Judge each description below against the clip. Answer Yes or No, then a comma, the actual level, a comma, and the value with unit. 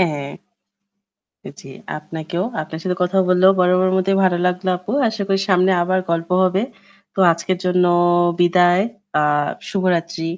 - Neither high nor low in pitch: Yes, medium, 180 Hz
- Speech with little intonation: Yes, narrow, 1.9 semitones